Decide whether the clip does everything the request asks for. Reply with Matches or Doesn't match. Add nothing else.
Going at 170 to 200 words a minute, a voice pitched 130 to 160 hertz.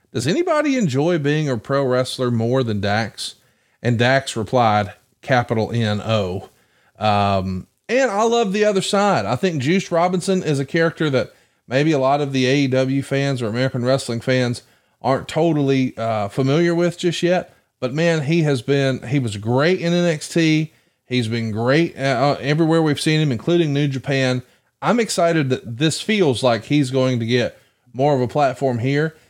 Matches